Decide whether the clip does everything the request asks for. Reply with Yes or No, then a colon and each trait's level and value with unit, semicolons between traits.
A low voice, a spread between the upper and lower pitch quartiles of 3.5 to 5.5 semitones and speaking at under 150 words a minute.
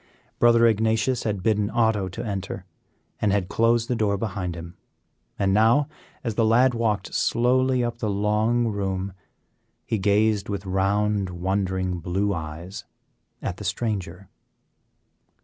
No: low, 105 Hz; average, 3.0 semitones; average, 140 wpm